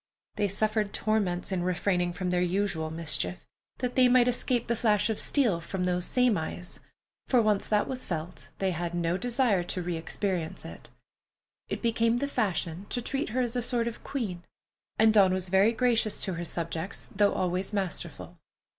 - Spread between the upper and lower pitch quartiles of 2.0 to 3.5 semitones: No, average, 4.7 semitones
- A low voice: No, high, 200 Hz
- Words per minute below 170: No, average, 180 wpm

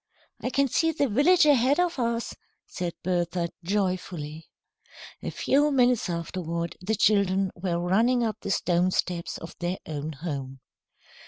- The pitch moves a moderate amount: No, wide, 6.2 semitones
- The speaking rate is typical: Yes, average, 145 wpm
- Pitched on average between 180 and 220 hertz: Yes, medium, 185 Hz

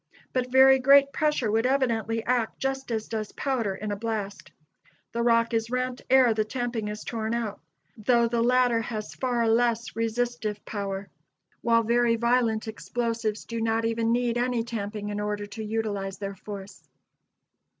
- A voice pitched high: Yes, high, 230 Hz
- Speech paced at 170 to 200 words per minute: No, average, 160 wpm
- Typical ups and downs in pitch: No, narrow, 2.1 semitones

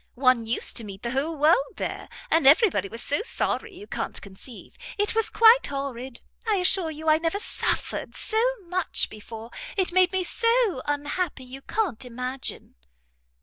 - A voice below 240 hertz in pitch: No, very high, 305 Hz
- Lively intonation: Yes, wide, 7.0 semitones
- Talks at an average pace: Yes, average, 170 wpm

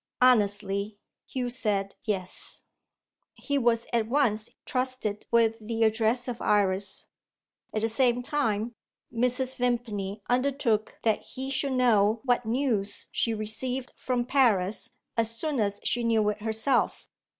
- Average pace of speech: No, slow, 130 wpm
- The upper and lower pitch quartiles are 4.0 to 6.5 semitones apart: No, average, 3.0 semitones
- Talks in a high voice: Yes, high, 230 Hz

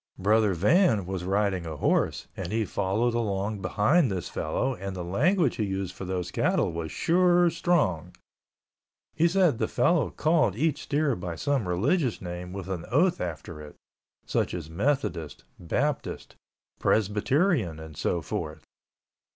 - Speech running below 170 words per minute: Yes, average, 150 wpm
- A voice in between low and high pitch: No, low, 100 Hz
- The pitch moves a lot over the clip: Yes, wide, 8.3 semitones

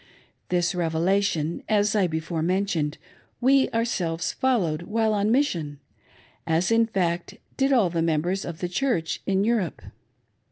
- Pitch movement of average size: Yes, average, 4.9 semitones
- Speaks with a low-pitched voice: No, medium, 185 Hz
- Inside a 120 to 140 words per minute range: Yes, slow, 135 wpm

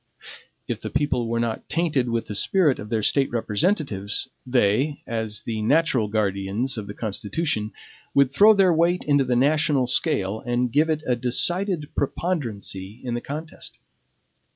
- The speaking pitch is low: Yes, low, 125 Hz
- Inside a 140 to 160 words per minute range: Yes, average, 155 wpm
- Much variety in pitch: Yes, wide, 5.8 semitones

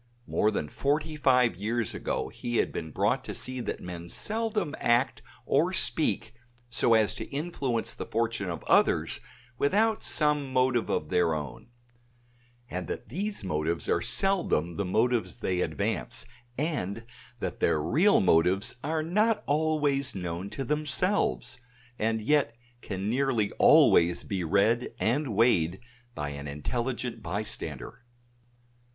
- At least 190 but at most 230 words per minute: No, slow, 135 wpm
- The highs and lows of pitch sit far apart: Yes, wide, 7.6 semitones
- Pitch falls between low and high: No, low, 115 Hz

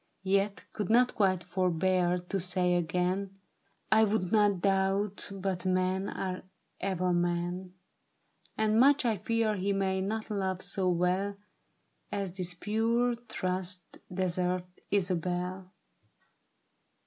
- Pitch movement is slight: Yes, narrow, 2.0 semitones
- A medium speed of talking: No, slow, 120 wpm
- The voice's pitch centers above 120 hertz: Yes, high, 190 Hz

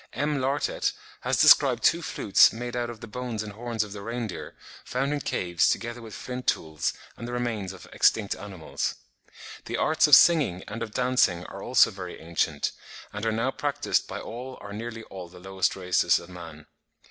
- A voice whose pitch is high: No, low, 110 Hz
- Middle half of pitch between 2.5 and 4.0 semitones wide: No, average, 4.6 semitones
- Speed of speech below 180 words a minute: No, average, 190 wpm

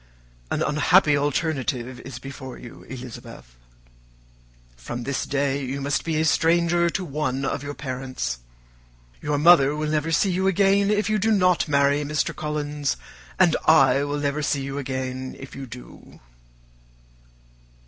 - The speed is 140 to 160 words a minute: Yes, average, 150 wpm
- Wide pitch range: No, average, 3.3 semitones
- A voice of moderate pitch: Yes, medium, 145 Hz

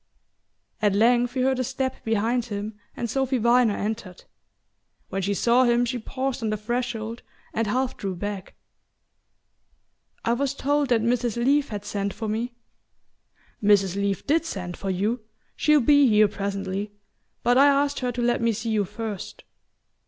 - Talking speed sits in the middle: Yes, average, 165 wpm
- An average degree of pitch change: Yes, average, 3.5 semitones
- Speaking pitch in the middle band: No, high, 230 Hz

